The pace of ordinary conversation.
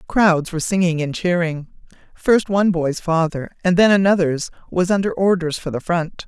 Yes: average, 170 wpm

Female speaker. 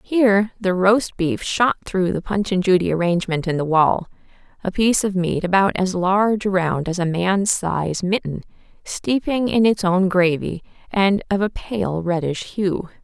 Yes: female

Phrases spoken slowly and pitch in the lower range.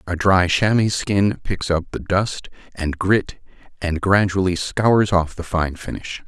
No: average, 165 wpm; very low, 90 Hz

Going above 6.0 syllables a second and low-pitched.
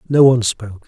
Yes: 7.1 syllables/s; low, 120 Hz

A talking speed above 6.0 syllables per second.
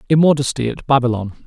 Yes: 6.8 syllables/s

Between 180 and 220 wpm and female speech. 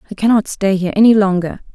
Yes: fast, 205 wpm; female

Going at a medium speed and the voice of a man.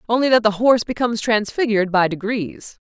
No: average, 165 wpm; female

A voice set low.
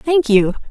No: very high, 255 Hz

